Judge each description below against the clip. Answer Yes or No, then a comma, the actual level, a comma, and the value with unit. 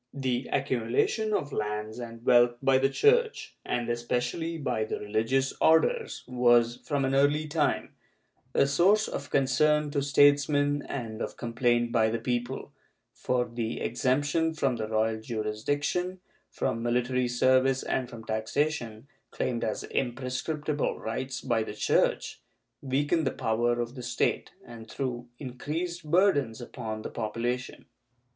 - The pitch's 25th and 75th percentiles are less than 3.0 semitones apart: No, average, 3.5 semitones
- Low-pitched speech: Yes, low, 125 Hz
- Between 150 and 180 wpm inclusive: No, average, 140 wpm